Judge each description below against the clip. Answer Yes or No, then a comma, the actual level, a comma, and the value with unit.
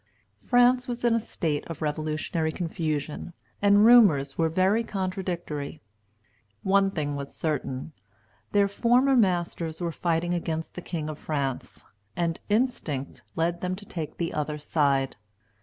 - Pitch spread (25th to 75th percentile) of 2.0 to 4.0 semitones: No, average, 4.5 semitones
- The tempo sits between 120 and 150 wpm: Yes, average, 140 wpm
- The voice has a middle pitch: Yes, medium, 170 Hz